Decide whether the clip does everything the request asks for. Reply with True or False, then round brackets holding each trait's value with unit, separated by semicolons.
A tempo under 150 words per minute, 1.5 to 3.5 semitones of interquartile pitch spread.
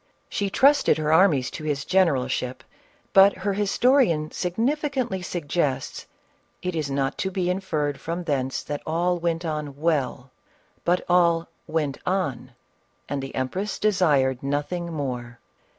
False (140 wpm; 4.8 semitones)